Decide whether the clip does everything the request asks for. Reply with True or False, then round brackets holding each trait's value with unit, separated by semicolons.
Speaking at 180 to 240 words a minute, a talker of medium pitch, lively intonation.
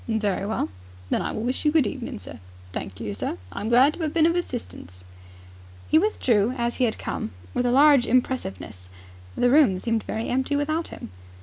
False (200 wpm; 245 Hz; 5.8 semitones)